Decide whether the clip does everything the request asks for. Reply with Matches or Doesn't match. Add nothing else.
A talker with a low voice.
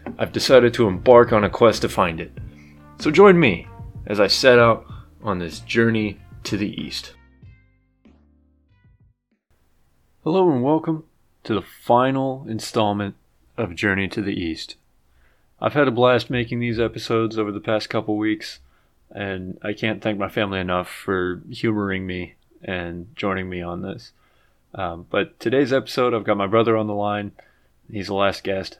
Matches